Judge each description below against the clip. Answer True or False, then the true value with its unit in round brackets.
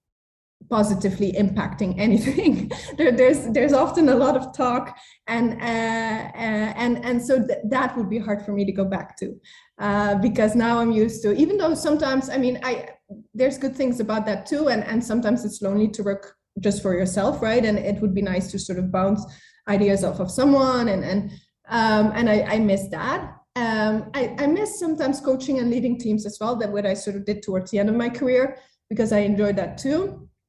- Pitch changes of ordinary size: True (4.0 semitones)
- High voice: True (225 Hz)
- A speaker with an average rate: False (210 wpm)